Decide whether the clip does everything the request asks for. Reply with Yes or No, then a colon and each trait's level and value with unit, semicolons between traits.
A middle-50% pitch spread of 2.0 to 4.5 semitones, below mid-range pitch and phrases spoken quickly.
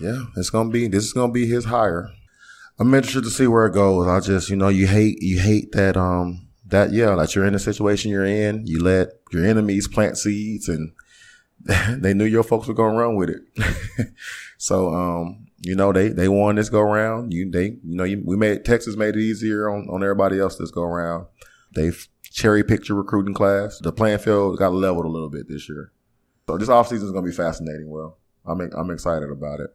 Yes: average, 3.3 semitones; low, 100 Hz; fast, 230 wpm